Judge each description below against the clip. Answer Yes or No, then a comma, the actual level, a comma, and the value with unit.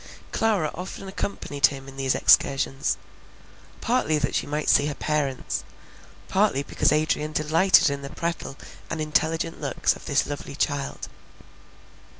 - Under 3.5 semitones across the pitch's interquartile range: Yes, average, 2.8 semitones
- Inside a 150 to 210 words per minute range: No, average, 140 wpm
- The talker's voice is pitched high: No, medium, 150 Hz